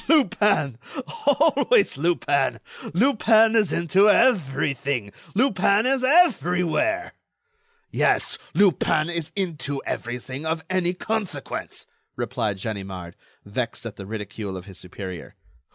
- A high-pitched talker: No, medium, 170 Hz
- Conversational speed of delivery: No, slow, 105 wpm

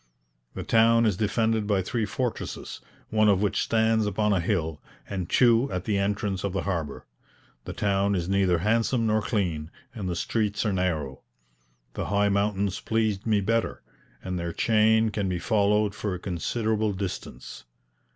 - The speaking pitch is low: Yes, low, 100 Hz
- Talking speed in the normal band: Yes, average, 165 wpm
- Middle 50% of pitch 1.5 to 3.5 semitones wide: Yes, average, 2.8 semitones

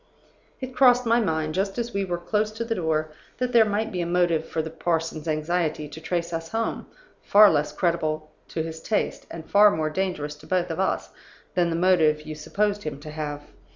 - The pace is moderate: No, fast, 210 wpm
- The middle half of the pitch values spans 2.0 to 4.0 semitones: No, average, 4.7 semitones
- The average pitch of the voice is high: No, medium, 170 Hz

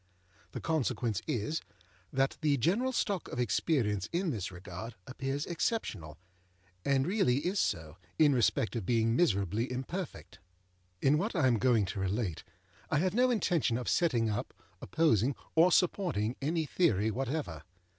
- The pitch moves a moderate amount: No, wide, 7.2 semitones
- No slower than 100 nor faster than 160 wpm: Yes, average, 145 wpm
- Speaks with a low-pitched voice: Yes, low, 130 Hz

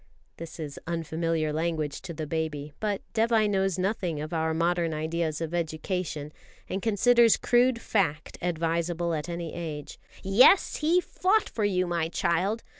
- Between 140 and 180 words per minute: Yes, average, 150 wpm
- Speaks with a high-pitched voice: No, medium, 170 Hz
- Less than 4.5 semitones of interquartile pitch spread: Yes, average, 3.7 semitones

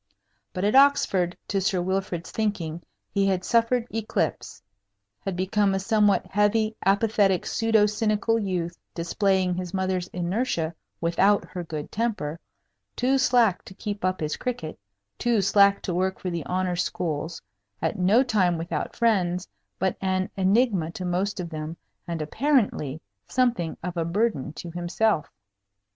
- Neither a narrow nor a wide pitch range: Yes, average, 3.5 semitones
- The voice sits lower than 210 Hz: Yes, high, 190 Hz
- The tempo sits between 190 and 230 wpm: No, average, 145 wpm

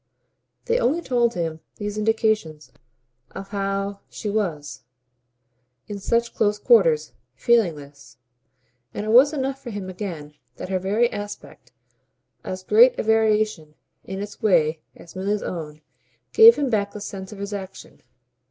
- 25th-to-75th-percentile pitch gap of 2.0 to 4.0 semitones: Yes, average, 3.4 semitones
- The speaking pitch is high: Yes, high, 205 Hz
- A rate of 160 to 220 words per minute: No, average, 145 wpm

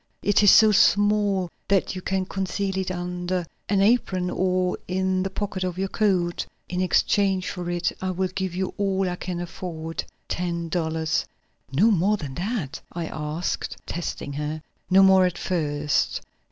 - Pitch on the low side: No, medium, 185 Hz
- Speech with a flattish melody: Yes, narrow, 1.9 semitones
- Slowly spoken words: No, average, 165 wpm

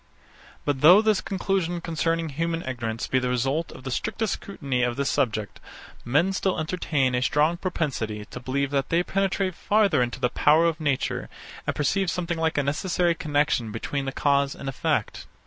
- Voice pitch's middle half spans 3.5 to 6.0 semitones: Yes, average, 4.7 semitones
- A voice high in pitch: No, medium, 150 Hz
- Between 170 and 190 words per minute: Yes, average, 180 wpm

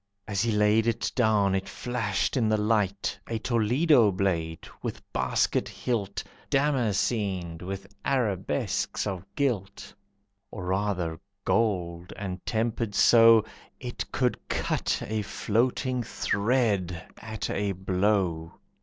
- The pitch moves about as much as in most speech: Yes, average, 3.4 semitones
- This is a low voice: Yes, low, 105 Hz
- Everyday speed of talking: No, slow, 115 wpm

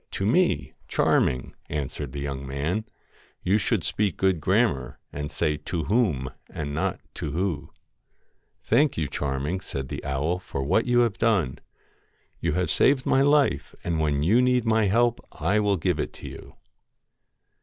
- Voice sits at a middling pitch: No, very low, 90 Hz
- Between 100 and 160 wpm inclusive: No, average, 180 wpm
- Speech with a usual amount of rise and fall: No, wide, 7.3 semitones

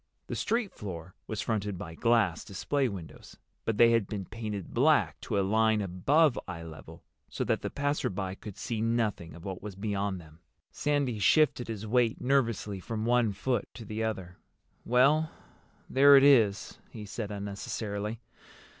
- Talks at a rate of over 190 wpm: No, average, 165 wpm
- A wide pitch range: No, average, 3.7 semitones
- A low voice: Yes, low, 110 Hz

